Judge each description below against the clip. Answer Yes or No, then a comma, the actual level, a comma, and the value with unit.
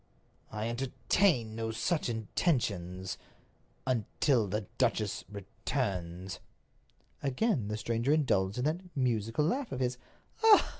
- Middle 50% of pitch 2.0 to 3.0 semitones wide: No, average, 4.4 semitones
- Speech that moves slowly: Yes, slow, 100 wpm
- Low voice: Yes, low, 115 Hz